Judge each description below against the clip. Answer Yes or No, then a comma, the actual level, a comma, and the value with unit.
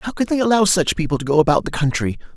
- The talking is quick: Yes, fast, 280 wpm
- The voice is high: No, medium, 170 Hz